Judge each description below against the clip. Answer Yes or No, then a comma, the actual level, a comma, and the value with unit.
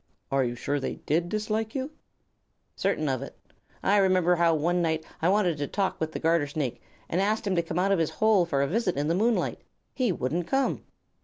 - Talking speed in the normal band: No, fast, 220 wpm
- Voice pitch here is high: No, medium, 175 Hz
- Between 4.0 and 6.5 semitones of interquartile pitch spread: Yes, average, 4.5 semitones